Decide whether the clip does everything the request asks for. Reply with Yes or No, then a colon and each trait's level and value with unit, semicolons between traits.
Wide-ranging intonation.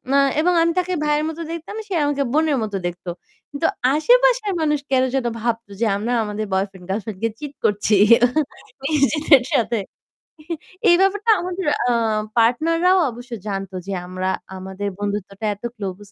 Yes: wide, 7.9 semitones